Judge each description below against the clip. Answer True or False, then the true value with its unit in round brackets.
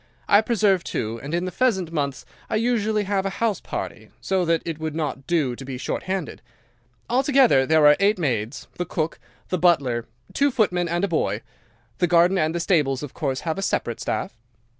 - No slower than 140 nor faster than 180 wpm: False (200 wpm)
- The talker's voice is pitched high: False (170 Hz)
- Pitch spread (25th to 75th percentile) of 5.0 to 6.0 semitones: True (5.3 semitones)